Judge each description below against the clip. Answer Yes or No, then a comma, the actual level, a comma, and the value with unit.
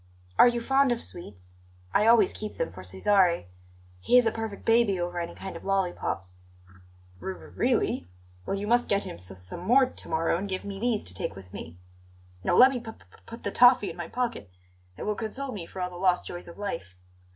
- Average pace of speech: No, fast, 220 wpm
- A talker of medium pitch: No, high, 195 Hz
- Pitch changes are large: Yes, wide, 6.1 semitones